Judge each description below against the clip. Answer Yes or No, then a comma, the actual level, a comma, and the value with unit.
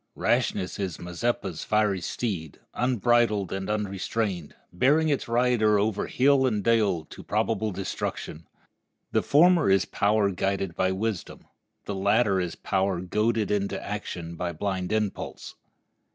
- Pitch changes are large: No, average, 3.3 semitones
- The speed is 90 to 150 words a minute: Yes, slow, 135 wpm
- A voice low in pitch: Yes, low, 100 Hz